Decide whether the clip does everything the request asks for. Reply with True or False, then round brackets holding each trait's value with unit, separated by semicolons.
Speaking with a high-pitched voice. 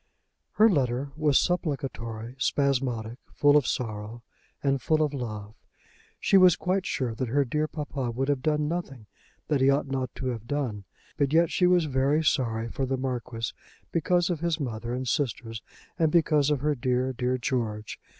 False (135 Hz)